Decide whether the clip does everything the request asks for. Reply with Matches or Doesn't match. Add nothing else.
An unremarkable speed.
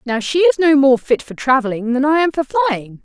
Doesn't match